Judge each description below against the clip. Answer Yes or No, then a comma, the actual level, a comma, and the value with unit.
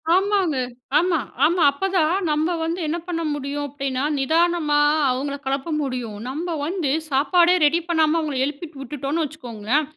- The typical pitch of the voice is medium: No, very high, 305 Hz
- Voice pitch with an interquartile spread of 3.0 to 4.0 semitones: Yes, average, 3.7 semitones